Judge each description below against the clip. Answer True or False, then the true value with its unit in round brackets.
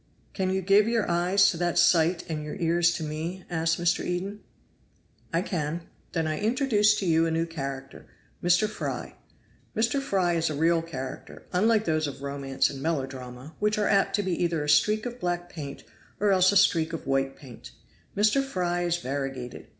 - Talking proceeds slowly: False (190 wpm)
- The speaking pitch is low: False (170 Hz)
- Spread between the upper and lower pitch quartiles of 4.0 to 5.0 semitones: True (4.3 semitones)